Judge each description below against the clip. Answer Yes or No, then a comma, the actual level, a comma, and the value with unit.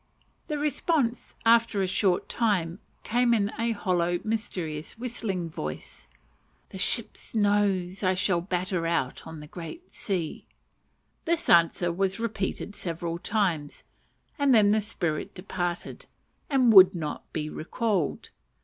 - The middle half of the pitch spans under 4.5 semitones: No, average, 4.8 semitones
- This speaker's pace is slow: Yes, slow, 130 wpm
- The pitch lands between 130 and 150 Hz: No, high, 190 Hz